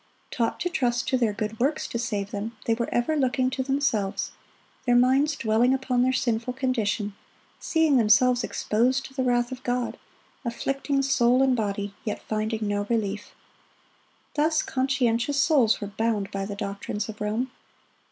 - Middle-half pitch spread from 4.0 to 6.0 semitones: No, average, 3.5 semitones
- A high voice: Yes, high, 240 Hz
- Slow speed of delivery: No, average, 160 wpm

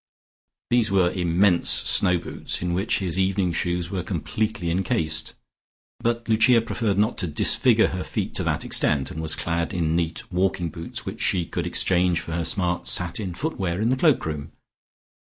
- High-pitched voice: No, very low, 90 Hz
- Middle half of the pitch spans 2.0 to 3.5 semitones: Yes, average, 3.2 semitones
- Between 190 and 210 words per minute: No, average, 175 wpm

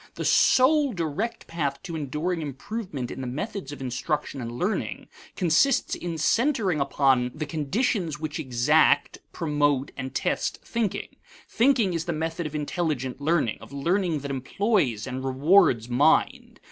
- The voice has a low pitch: No, medium, 155 Hz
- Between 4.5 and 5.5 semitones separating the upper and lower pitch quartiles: Yes, average, 5.2 semitones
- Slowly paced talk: No, average, 145 wpm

